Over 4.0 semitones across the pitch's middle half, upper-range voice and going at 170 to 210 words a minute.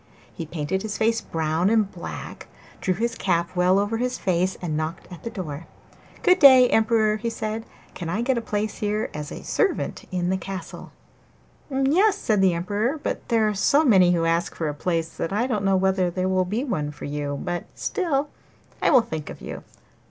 Yes: average, 4.9 semitones; high, 195 Hz; average, 200 wpm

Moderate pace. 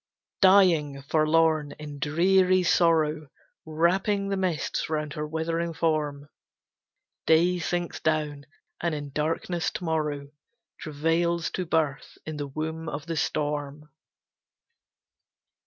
No: slow, 110 wpm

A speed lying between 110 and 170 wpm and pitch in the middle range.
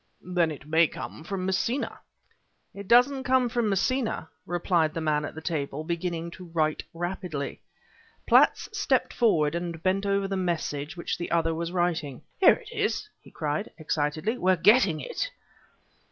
Yes: average, 160 wpm; medium, 175 Hz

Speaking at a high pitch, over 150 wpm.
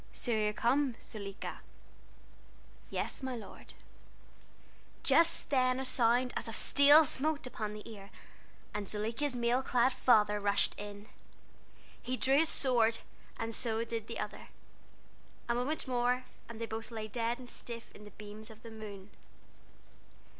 No: high, 230 Hz; average, 145 wpm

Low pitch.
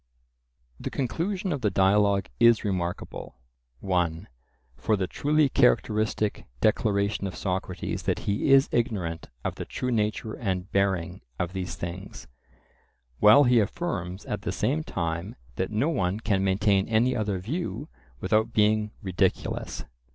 Yes: low, 100 Hz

